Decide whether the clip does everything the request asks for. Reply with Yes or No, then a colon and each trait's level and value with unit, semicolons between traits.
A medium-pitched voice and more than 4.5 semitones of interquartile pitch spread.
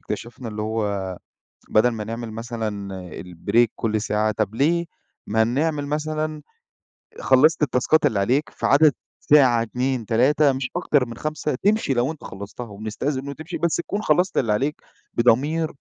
No: low, 125 Hz; wide, 5.5 semitones